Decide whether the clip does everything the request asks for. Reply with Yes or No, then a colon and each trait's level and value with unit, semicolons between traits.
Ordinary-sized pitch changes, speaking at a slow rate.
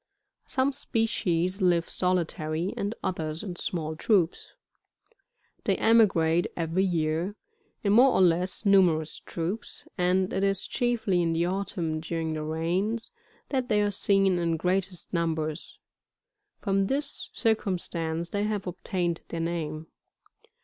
Yes: average, 3.3 semitones; slow, 130 wpm